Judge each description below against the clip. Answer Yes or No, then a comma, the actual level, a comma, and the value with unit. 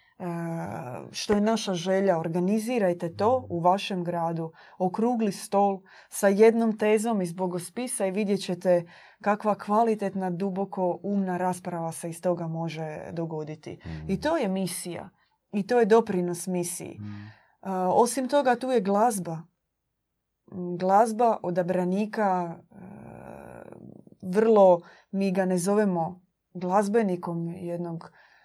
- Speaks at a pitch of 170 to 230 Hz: Yes, medium, 185 Hz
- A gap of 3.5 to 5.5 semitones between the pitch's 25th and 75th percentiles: No, average, 3.0 semitones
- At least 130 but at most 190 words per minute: No, slow, 110 wpm